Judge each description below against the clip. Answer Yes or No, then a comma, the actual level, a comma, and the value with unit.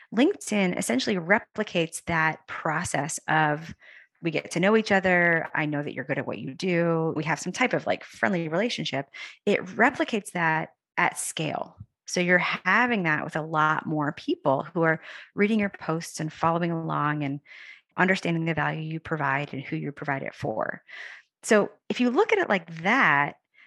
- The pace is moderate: Yes, average, 180 wpm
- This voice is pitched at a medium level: Yes, medium, 165 Hz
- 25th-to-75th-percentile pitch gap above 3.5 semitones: Yes, average, 4.6 semitones